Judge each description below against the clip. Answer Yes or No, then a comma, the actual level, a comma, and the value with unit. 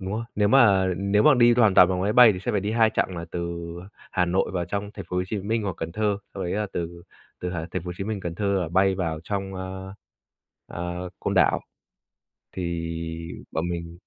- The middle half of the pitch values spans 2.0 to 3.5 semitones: Yes, average, 2.9 semitones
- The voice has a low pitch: Yes, very low, 95 Hz